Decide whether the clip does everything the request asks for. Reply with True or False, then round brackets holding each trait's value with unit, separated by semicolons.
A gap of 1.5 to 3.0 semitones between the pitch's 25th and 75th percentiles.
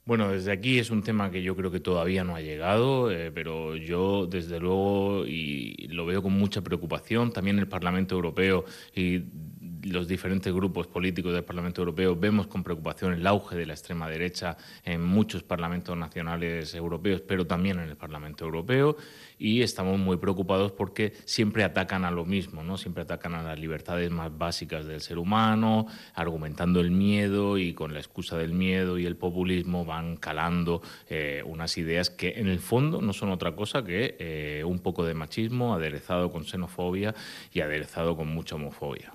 True (2.6 semitones)